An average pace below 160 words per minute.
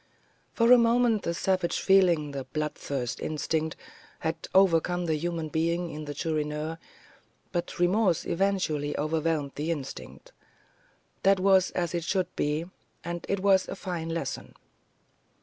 Yes: slow, 135 wpm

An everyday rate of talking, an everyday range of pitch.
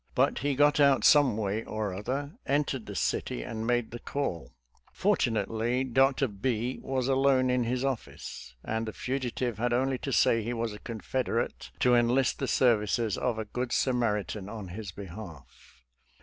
Yes: average, 170 wpm; average, 3.5 semitones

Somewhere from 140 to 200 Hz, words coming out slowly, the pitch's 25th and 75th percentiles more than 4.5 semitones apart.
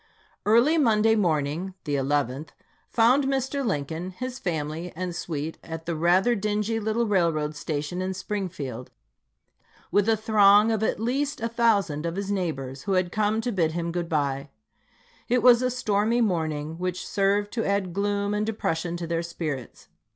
No: high, 190 Hz; average, 165 wpm; average, 5.3 semitones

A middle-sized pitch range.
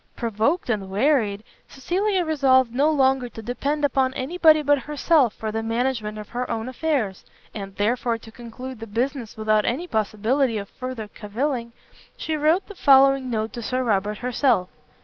Yes: average, 4.2 semitones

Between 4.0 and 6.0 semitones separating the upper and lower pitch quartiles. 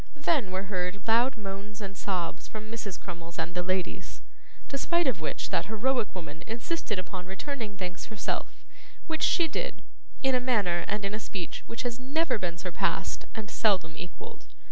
Yes: average, 4.6 semitones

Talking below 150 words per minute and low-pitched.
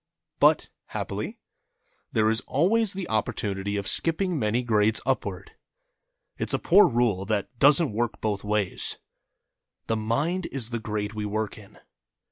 Yes: average, 140 wpm; low, 110 Hz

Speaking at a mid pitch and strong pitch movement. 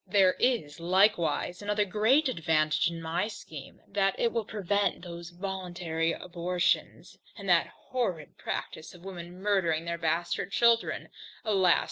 No: medium, 180 Hz; average, 3.3 semitones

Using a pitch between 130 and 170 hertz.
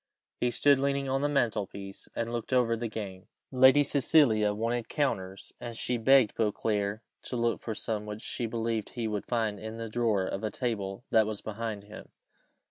No: low, 115 Hz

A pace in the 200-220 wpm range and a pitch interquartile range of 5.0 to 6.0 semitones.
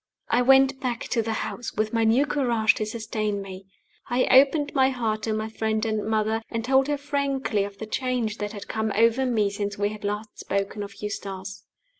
No: fast, 205 wpm; average, 3.3 semitones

